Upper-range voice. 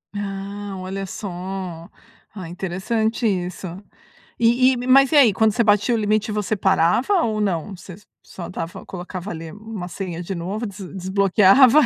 Yes: high, 200 Hz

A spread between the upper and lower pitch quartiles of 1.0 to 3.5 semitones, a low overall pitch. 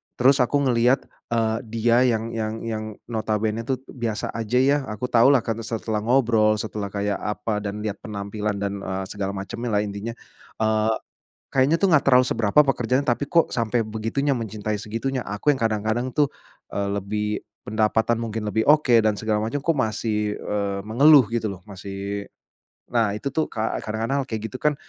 Yes: average, 2.8 semitones; low, 110 Hz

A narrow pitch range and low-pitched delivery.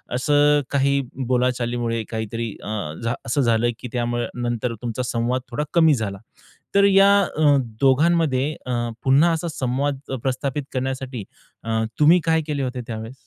No: average, 3.6 semitones; low, 130 Hz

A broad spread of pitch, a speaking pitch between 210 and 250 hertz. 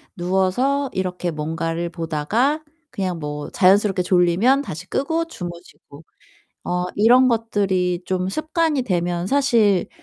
No: wide, 6.2 semitones; medium, 185 Hz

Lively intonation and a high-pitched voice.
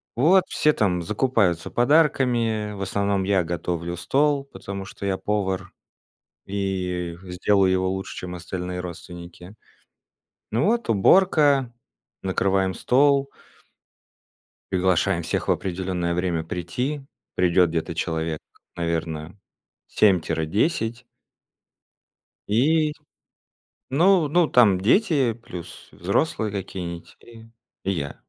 No: wide, 5.8 semitones; very low, 95 Hz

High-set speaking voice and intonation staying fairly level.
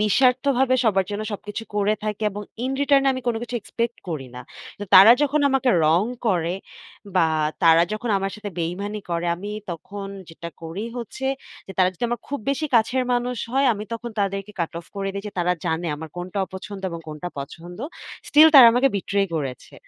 No: high, 205 Hz; wide, 5.5 semitones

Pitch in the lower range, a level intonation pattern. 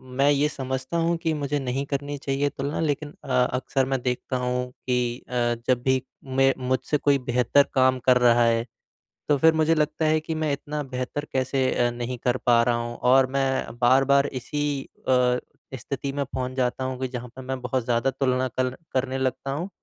Yes: low, 130 Hz; narrow, 2.1 semitones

